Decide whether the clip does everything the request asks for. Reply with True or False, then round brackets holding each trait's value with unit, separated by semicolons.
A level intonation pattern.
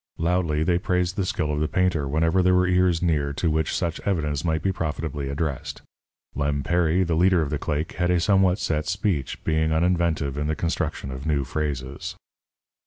False (3.3 semitones)